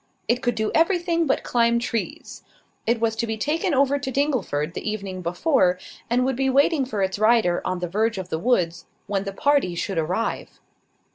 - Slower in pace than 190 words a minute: No, average, 195 wpm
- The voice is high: Yes, high, 230 Hz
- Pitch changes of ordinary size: No, wide, 6.1 semitones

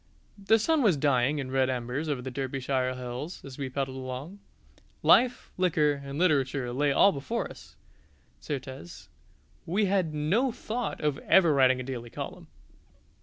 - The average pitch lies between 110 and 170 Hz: Yes, medium, 140 Hz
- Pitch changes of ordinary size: Yes, average, 5.0 semitones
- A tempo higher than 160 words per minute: No, average, 155 wpm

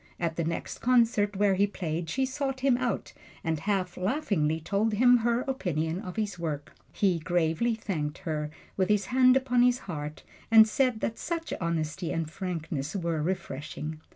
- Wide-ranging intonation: Yes, wide, 6.6 semitones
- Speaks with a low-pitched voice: No, high, 190 Hz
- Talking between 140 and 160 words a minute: No, average, 170 wpm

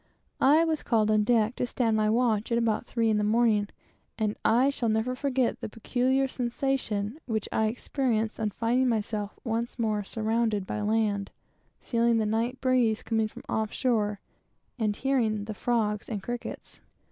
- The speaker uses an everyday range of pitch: No, narrow, 2.3 semitones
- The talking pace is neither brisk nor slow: Yes, average, 170 wpm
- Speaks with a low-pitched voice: No, high, 225 Hz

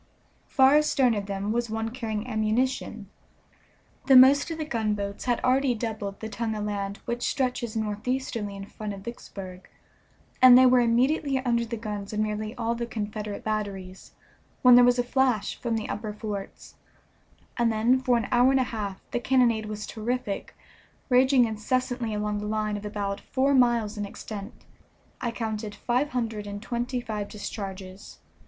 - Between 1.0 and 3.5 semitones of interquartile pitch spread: Yes, average, 3.0 semitones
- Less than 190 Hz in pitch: No, high, 225 Hz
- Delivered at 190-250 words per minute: No, average, 170 wpm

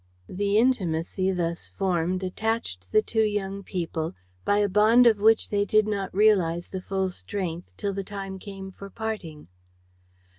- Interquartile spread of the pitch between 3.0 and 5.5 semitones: No, narrow, 2.6 semitones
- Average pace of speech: Yes, average, 155 wpm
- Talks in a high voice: Yes, high, 195 Hz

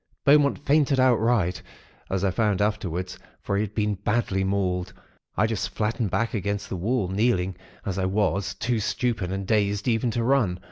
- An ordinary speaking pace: Yes, average, 175 wpm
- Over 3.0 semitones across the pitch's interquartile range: Yes, average, 3.5 semitones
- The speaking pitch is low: Yes, low, 105 Hz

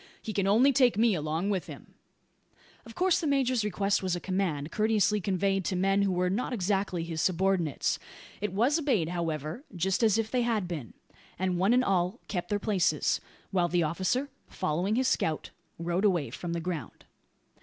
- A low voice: No, high, 190 Hz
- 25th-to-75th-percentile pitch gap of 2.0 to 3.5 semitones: No, average, 3.9 semitones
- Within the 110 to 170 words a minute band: No, average, 185 wpm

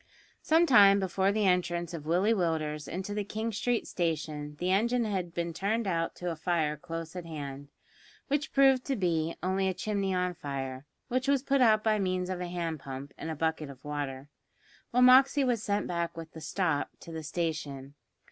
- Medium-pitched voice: Yes, medium, 180 Hz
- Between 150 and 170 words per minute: No, average, 200 wpm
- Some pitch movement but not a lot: Yes, average, 4.9 semitones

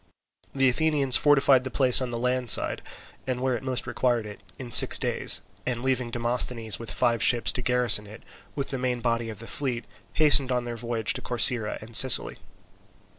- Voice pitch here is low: Yes, low, 125 Hz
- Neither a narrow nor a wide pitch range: No, narrow, 1.8 semitones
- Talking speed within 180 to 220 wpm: Yes, average, 190 wpm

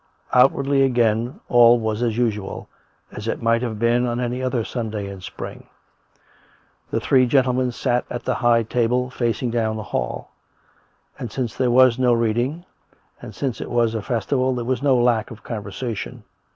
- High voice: No, low, 120 Hz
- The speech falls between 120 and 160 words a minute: No, average, 175 wpm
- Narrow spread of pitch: Yes, narrow, 1.9 semitones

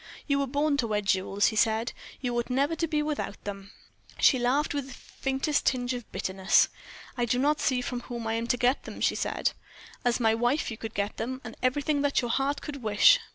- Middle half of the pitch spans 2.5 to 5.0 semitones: Yes, average, 3.9 semitones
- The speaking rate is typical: No, fast, 225 wpm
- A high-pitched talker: Yes, very high, 250 Hz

